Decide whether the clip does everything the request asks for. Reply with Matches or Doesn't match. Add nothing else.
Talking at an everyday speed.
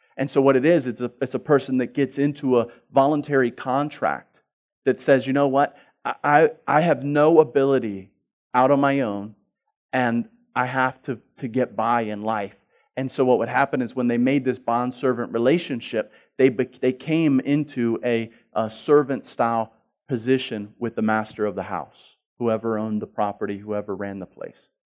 Matches